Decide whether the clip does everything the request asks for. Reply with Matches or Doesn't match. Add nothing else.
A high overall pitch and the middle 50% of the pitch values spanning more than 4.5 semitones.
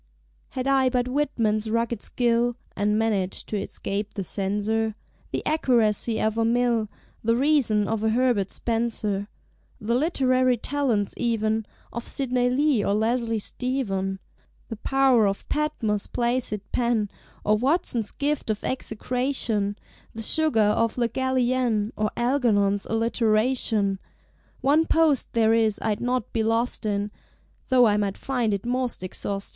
Doesn't match